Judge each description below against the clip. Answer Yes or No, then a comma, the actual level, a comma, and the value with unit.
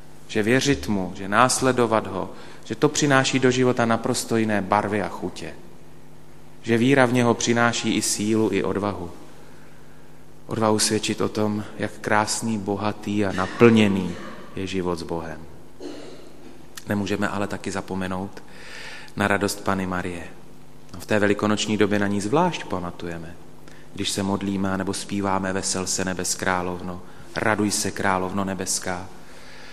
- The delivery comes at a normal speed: Yes, average, 135 wpm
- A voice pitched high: No, low, 100 Hz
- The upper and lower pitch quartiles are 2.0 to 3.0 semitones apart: Yes, average, 2.7 semitones